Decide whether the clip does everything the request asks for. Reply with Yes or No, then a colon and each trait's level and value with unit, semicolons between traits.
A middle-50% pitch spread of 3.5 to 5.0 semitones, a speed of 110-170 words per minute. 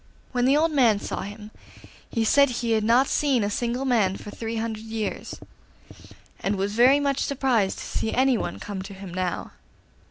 No: average, 4.0 semitones; average, 185 wpm